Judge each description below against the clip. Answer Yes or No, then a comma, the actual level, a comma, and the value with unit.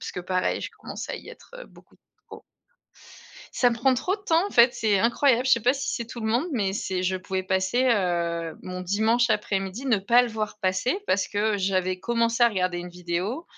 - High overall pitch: Yes, high, 210 Hz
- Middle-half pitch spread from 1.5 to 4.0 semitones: No, average, 4.5 semitones